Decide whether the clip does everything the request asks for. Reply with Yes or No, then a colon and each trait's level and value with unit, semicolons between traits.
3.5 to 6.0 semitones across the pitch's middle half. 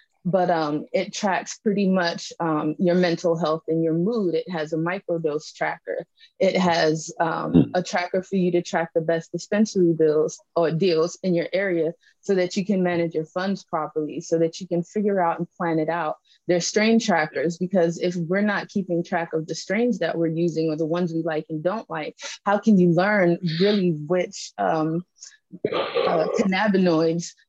No: narrow, 2.5 semitones